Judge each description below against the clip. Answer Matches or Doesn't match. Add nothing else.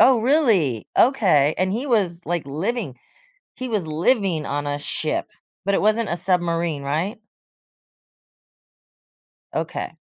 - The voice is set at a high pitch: Doesn't match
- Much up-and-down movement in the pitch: Matches